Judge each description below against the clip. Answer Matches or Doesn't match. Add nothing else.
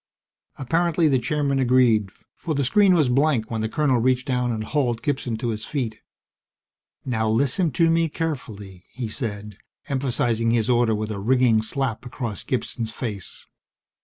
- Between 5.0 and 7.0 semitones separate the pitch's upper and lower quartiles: Doesn't match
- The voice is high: Doesn't match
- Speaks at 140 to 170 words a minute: Matches